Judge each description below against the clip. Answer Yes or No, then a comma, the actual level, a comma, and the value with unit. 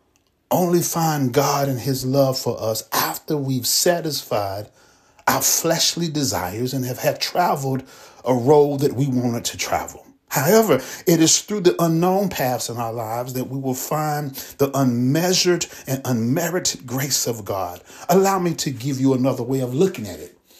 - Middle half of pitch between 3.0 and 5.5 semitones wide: Yes, average, 4.2 semitones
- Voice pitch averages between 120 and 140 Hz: Yes, low, 135 Hz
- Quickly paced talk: No, average, 165 wpm